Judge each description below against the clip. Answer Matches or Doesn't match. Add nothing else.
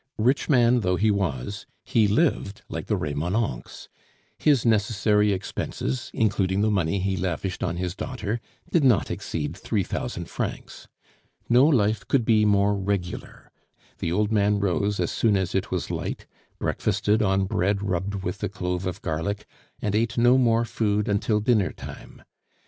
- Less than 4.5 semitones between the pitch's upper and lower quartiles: Matches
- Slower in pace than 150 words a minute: Doesn't match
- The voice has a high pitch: Doesn't match